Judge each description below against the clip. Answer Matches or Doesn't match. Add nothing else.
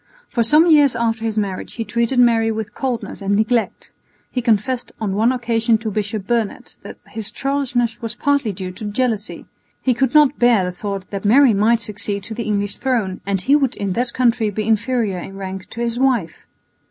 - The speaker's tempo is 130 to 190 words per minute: Doesn't match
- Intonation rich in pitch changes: Doesn't match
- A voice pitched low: Doesn't match